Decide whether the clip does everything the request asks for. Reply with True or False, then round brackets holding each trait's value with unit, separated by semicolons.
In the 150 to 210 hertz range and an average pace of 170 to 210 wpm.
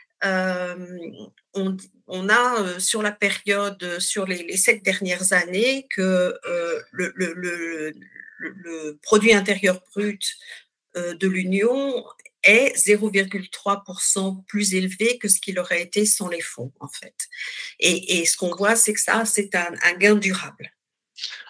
False (190 Hz; 150 wpm)